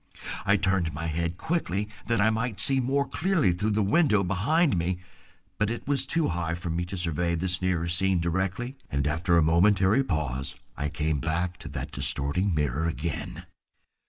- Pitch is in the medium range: No, very low, 90 Hz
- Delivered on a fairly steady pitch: No, average, 4.5 semitones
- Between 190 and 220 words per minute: No, average, 180 wpm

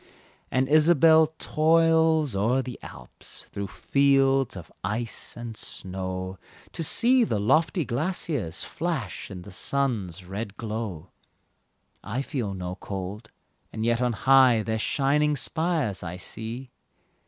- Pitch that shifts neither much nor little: No, wide, 7.0 semitones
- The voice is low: Yes, low, 120 Hz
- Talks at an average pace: No, slow, 125 wpm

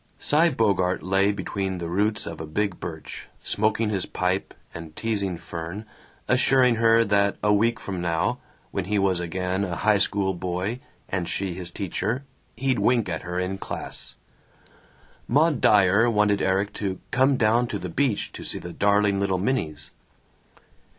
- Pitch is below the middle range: Yes, low, 100 Hz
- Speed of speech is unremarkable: Yes, average, 165 wpm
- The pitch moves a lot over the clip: No, average, 3.4 semitones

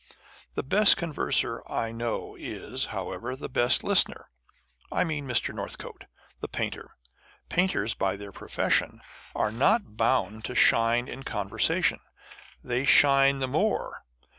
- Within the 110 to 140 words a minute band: Yes, slow, 135 wpm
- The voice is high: No, low, 125 Hz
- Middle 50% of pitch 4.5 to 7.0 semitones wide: No, average, 3.7 semitones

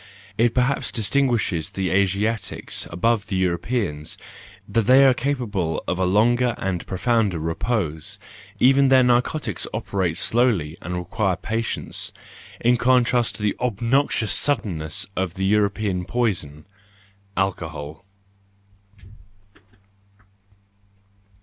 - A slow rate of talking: Yes, slow, 110 wpm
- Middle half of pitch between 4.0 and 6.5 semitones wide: Yes, average, 5.1 semitones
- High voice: No, low, 105 Hz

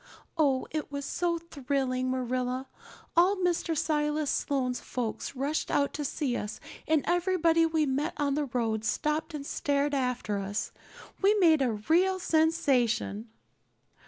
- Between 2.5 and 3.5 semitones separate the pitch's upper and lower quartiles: No, average, 4.1 semitones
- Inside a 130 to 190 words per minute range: Yes, average, 140 wpm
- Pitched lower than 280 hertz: No, very high, 285 Hz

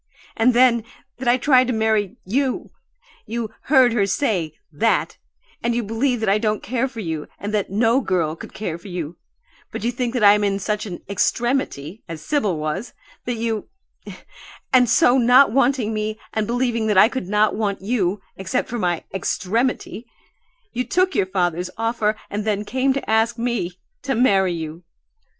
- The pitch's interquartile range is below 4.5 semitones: Yes, average, 4.0 semitones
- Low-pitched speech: No, high, 220 Hz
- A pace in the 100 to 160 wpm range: No, average, 175 wpm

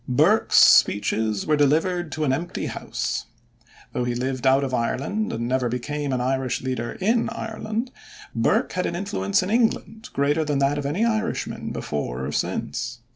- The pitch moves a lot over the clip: Yes, wide, 6.5 semitones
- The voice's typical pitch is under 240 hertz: Yes, medium, 140 Hz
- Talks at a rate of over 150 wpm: Yes, average, 170 wpm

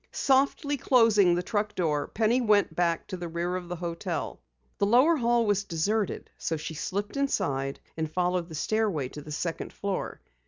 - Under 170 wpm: No, average, 180 wpm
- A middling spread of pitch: Yes, average, 4.9 semitones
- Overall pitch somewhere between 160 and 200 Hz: Yes, medium, 185 Hz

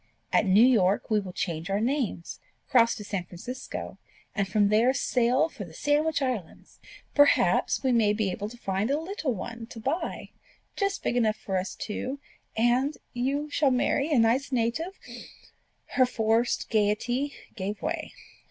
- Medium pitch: No, high, 235 Hz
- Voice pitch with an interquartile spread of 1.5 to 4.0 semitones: No, average, 4.7 semitones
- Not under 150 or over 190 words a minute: Yes, average, 165 wpm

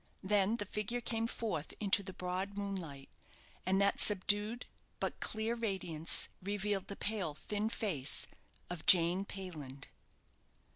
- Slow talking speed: Yes, slow, 130 wpm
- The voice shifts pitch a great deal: No, average, 2.7 semitones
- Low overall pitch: No, high, 200 Hz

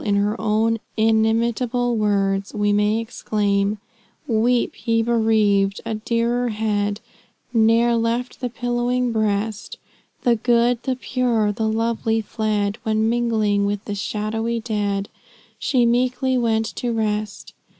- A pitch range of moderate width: No, narrow, 2.1 semitones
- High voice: Yes, high, 225 Hz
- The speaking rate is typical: No, slow, 125 wpm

